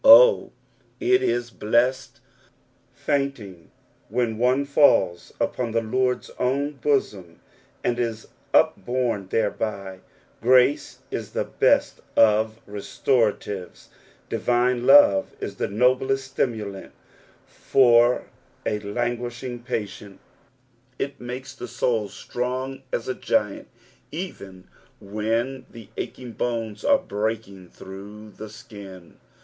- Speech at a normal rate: No, slow, 105 wpm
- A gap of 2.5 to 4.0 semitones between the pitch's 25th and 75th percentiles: Yes, average, 3.6 semitones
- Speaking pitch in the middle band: No, low, 120 Hz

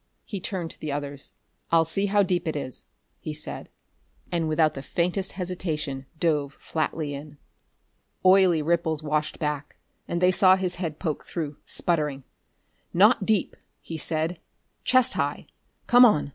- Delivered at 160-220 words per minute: No, average, 150 wpm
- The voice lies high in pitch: No, medium, 165 Hz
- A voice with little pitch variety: No, average, 3.4 semitones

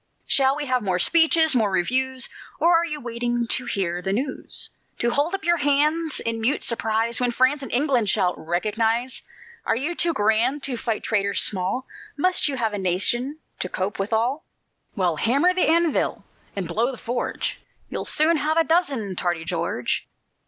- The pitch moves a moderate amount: No, wide, 6.0 semitones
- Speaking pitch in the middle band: No, high, 245 Hz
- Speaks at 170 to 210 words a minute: Yes, average, 175 wpm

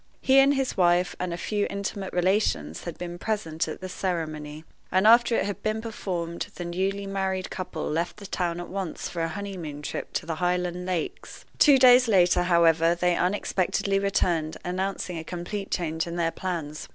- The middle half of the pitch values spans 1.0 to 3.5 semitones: Yes, average, 2.8 semitones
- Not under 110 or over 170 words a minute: No, average, 185 wpm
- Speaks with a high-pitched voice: No, medium, 180 Hz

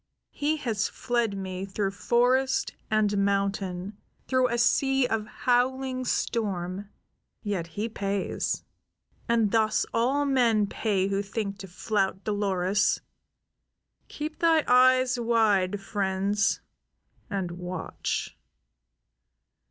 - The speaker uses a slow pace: Yes, slow, 105 wpm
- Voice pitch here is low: No, high, 210 Hz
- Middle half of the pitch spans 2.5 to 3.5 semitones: No, average, 3.9 semitones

